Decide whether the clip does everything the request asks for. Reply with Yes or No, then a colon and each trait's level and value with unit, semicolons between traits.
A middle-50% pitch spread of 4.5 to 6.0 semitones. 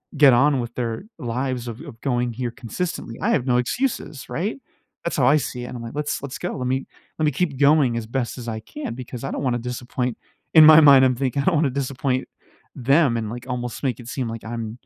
No: average, 2.8 semitones